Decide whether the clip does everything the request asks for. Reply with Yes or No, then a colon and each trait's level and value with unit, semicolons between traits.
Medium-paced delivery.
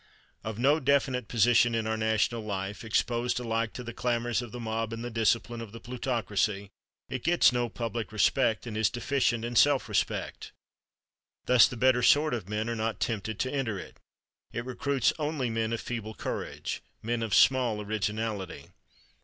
Yes: average, 175 wpm